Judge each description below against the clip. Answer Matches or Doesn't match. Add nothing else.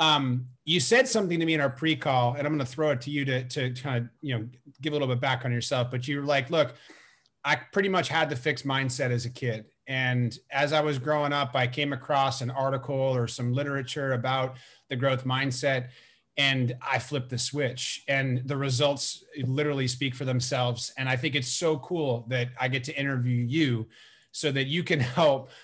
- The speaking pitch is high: Doesn't match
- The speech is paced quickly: Matches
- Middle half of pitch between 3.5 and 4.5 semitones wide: Doesn't match